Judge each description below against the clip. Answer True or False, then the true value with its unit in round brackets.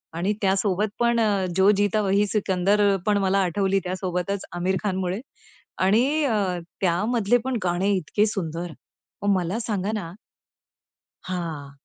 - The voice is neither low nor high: False (195 Hz)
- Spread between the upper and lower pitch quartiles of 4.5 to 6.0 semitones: False (2.6 semitones)